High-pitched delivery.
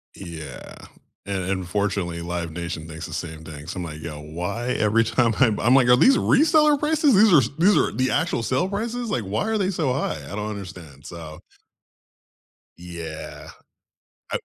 No: low, 100 Hz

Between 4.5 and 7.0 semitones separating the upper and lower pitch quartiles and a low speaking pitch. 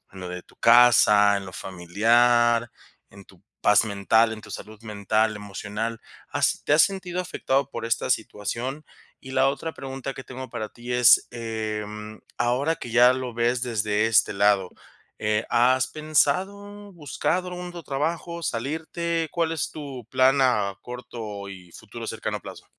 Yes: average, 4.8 semitones; low, 120 Hz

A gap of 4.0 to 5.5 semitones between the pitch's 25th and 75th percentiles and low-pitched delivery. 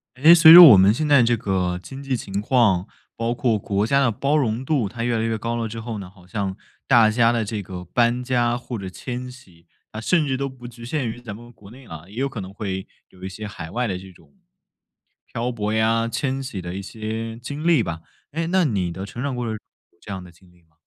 Yes: average, 4.3 semitones; low, 115 Hz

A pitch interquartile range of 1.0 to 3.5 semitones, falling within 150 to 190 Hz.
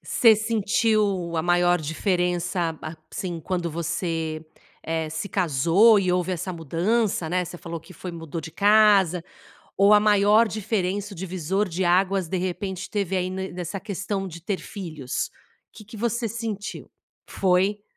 Yes: average, 3.2 semitones; medium, 185 Hz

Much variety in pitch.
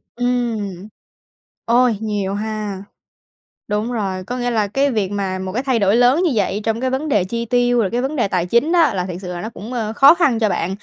No: average, 3.7 semitones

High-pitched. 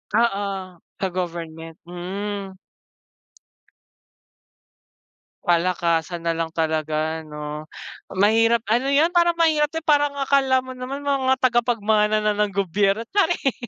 Yes: high, 205 Hz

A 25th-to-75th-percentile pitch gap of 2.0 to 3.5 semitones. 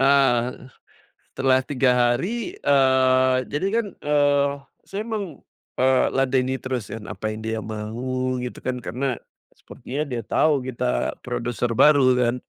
Yes: narrow, 2.4 semitones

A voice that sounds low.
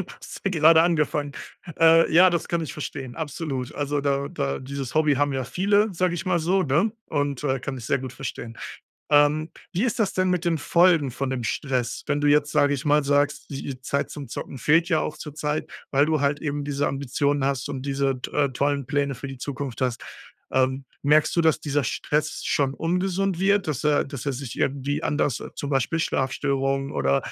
No: medium, 145 Hz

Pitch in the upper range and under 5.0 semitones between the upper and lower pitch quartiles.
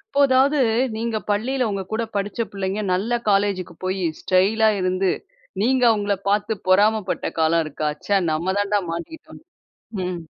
Yes: high, 205 Hz; average, 3.3 semitones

